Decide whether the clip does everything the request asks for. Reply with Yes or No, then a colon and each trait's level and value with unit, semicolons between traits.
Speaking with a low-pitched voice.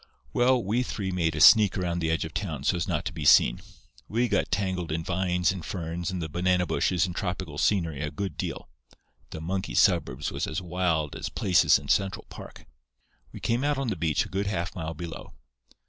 Yes: very low, 90 Hz